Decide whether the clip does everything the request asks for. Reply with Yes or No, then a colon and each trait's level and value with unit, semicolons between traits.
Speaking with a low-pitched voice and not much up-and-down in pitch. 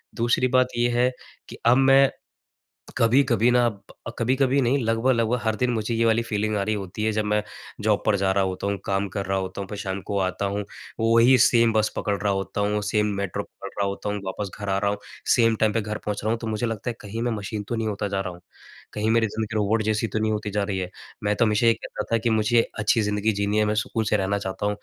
Yes: low, 105 Hz; narrow, 2.2 semitones